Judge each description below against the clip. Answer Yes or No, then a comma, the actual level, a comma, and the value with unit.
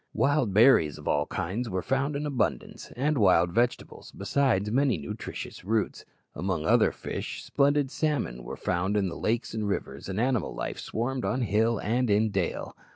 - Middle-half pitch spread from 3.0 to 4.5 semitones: No, wide, 5.5 semitones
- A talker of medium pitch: No, low, 110 Hz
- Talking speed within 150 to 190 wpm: Yes, average, 170 wpm